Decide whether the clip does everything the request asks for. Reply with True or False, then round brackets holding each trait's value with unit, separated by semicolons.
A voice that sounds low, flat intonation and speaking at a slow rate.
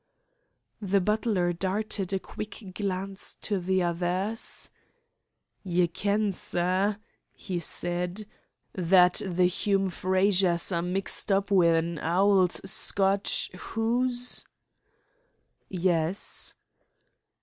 False (190 Hz; 2.2 semitones; 95 wpm)